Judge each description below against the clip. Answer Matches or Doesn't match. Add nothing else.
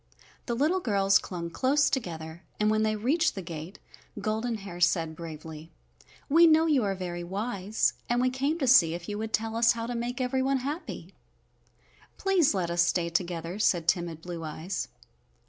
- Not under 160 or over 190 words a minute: Matches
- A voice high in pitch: Matches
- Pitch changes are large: Matches